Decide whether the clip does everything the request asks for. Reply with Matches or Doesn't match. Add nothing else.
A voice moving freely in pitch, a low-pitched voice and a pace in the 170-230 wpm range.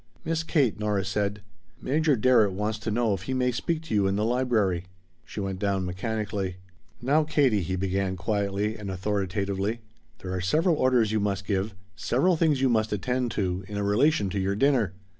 Doesn't match